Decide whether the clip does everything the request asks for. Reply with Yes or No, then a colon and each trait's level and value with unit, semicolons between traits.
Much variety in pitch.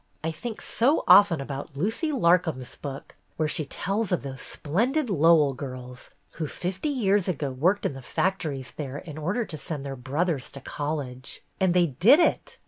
Yes: wide, 5.8 semitones